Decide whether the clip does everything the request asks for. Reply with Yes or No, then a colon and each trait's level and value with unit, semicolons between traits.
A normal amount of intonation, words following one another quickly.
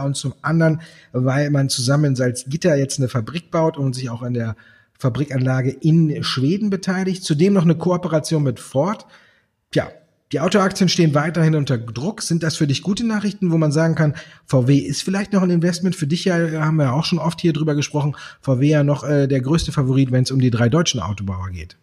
Yes: average, 3.9 semitones; fast, 210 wpm